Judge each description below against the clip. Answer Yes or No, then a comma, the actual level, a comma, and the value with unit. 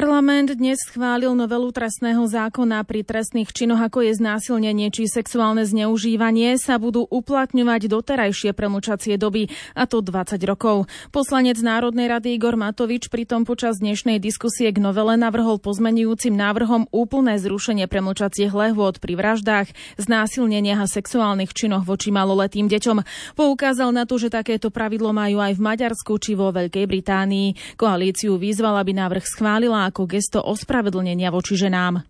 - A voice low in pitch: No, high, 220 Hz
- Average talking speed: Yes, average, 140 wpm